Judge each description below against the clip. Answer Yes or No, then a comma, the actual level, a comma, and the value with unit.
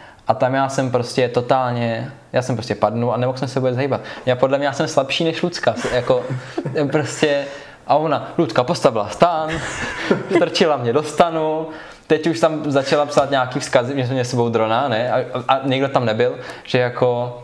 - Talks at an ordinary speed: No, fast, 195 wpm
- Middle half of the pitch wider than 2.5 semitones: Yes, average, 2.9 semitones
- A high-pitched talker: No, low, 135 Hz